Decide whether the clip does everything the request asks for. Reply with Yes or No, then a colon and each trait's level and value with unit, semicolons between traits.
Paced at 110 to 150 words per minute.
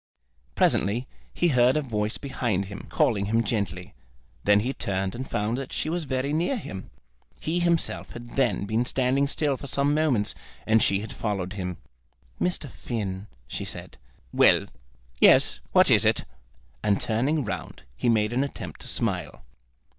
No: average, 160 wpm